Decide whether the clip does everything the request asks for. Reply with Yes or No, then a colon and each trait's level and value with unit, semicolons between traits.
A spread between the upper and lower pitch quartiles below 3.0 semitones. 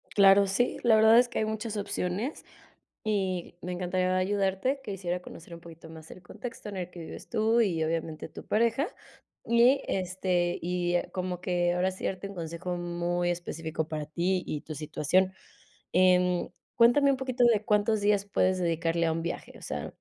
No: average, 3.3 semitones